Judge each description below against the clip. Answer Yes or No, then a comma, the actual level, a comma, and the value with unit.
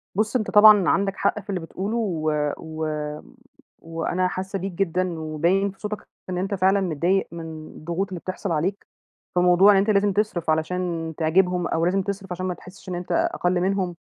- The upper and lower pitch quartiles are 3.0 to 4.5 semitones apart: No, narrow, 2.6 semitones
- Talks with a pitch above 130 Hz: Yes, medium, 185 Hz